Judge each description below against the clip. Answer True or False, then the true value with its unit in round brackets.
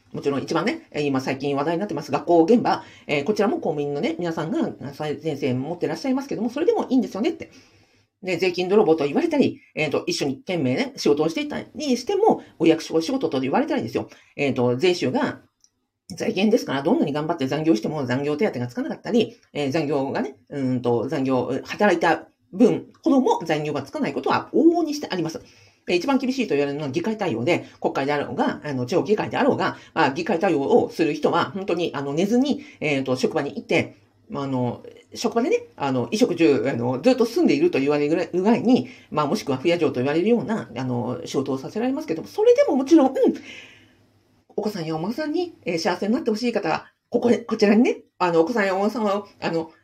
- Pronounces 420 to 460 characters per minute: True (430 characters per minute)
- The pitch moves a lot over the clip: True (8.8 semitones)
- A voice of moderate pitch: True (180 Hz)